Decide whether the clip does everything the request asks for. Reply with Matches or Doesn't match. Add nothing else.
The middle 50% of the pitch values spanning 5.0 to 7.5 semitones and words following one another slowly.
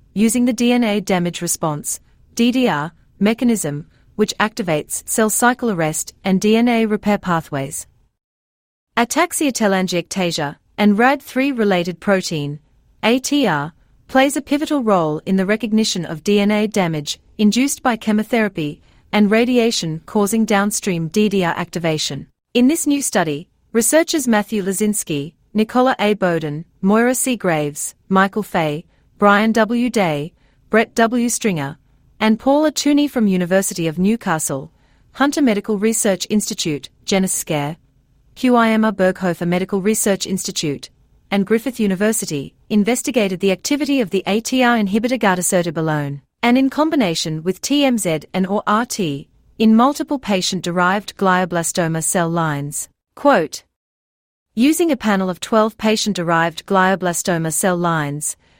Matches